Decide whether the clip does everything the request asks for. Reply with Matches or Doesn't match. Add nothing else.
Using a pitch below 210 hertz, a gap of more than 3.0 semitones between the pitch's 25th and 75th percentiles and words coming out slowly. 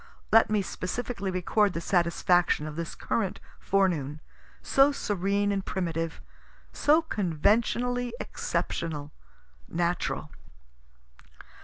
Matches